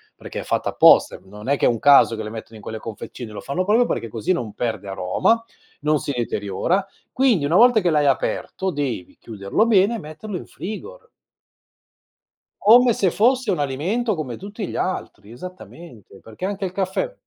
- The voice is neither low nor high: Yes, medium, 160 Hz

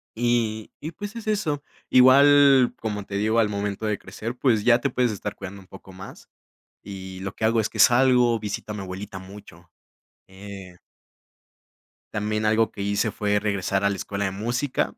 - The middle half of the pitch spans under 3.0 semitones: No, average, 3.4 semitones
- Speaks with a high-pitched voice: No, low, 105 Hz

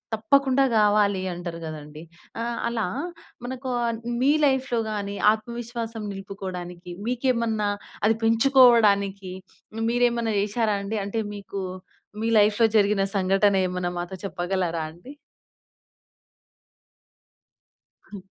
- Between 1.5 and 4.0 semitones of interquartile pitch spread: Yes, average, 3.5 semitones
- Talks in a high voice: Yes, high, 210 Hz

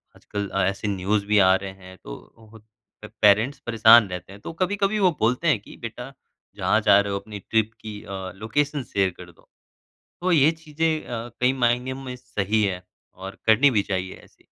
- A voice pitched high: No, low, 110 Hz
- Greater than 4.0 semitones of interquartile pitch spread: Yes, average, 4.8 semitones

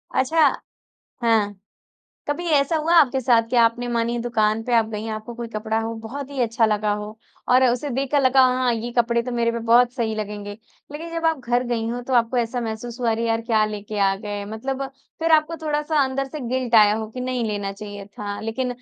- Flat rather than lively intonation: No, average, 3.0 semitones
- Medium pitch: No, high, 235 Hz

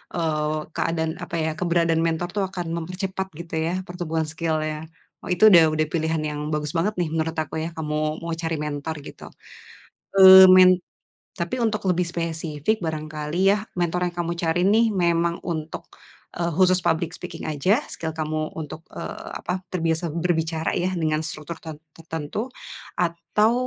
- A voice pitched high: No, medium, 165 Hz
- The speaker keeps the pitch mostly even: Yes, narrow, 2.0 semitones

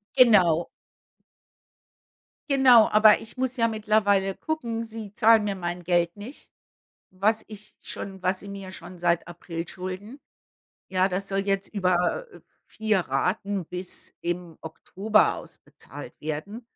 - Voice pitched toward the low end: No, high, 200 Hz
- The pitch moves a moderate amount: Yes, average, 3.4 semitones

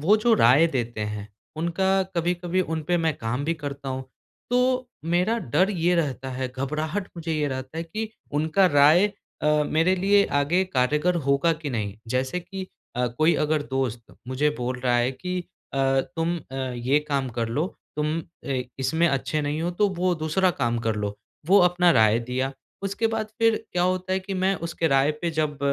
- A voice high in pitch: No, medium, 155 Hz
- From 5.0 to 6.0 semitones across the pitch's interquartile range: Yes, average, 5.3 semitones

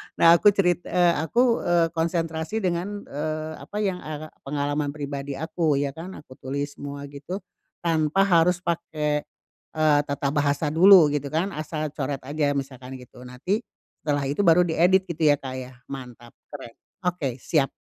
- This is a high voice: No, medium, 155 Hz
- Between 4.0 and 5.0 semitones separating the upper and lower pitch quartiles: No, average, 3.4 semitones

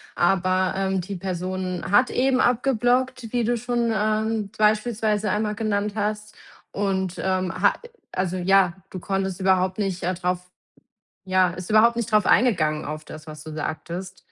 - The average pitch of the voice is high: Yes, high, 195 Hz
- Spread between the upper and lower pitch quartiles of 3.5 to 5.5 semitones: No, average, 2.9 semitones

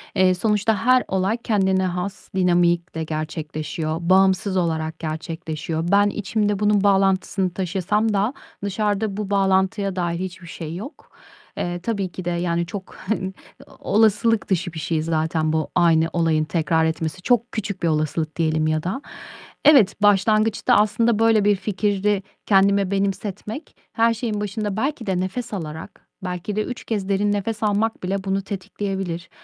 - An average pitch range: Yes, average, 3.4 semitones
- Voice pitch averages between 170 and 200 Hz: Yes, high, 190 Hz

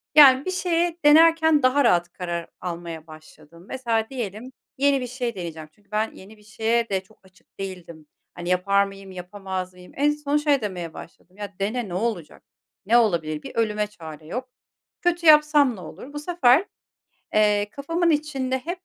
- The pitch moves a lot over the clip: Yes, wide, 7.6 semitones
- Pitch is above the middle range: Yes, high, 215 Hz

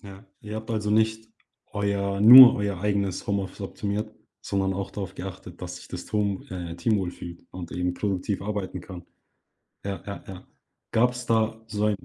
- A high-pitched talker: No, low, 100 Hz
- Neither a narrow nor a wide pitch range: No, narrow, 2.3 semitones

